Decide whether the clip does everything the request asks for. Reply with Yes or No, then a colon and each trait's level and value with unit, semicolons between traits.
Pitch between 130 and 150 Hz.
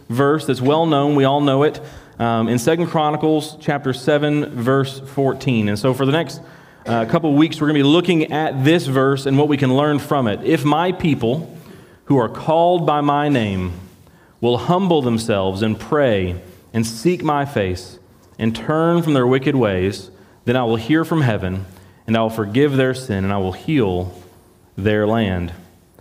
Yes: low, 135 Hz